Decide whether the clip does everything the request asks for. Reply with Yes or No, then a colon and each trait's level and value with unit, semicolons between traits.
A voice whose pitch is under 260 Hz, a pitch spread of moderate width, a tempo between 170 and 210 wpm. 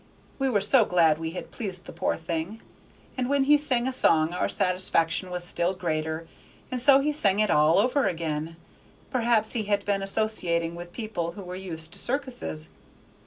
No: high, 190 Hz; wide, 6.3 semitones; average, 185 wpm